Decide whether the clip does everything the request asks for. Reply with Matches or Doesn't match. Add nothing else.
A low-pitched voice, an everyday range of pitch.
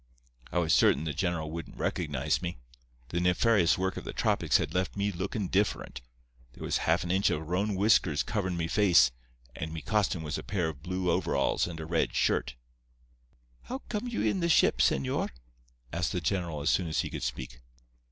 Matches